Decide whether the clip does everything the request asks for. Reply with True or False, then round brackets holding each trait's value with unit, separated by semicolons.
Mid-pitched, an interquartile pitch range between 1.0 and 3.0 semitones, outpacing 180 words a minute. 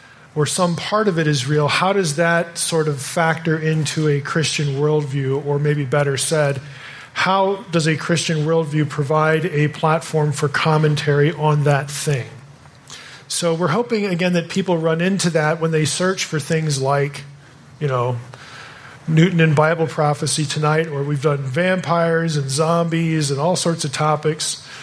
False (155 Hz; 2.4 semitones; 160 wpm)